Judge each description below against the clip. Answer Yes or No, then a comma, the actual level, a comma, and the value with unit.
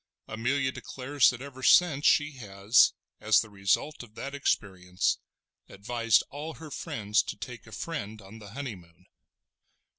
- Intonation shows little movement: No, wide, 5.5 semitones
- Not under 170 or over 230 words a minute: No, average, 145 wpm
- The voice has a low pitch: Yes, low, 115 Hz